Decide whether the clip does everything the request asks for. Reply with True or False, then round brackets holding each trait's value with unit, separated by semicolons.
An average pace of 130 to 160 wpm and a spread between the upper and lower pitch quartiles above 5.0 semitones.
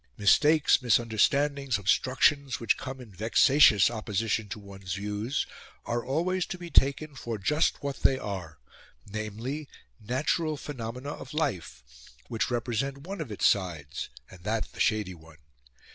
True (140 wpm; 5.4 semitones)